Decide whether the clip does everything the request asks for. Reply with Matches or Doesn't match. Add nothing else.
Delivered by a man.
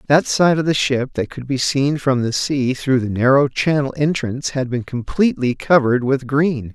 Matches